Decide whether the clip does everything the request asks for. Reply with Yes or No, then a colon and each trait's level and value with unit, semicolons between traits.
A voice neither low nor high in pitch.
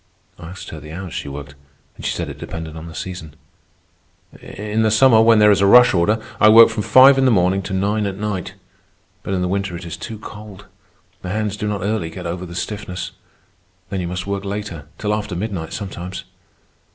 No: low, 100 Hz